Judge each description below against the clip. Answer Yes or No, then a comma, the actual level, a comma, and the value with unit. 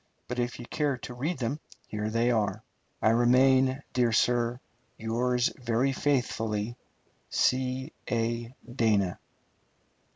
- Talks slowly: Yes, slow, 120 wpm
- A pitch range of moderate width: No, narrow, 2.2 semitones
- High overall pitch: No, low, 120 Hz